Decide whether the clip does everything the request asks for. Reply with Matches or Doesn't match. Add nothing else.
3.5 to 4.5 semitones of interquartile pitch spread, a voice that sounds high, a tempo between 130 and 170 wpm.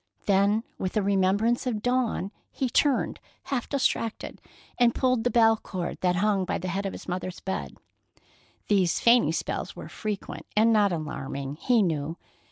Matches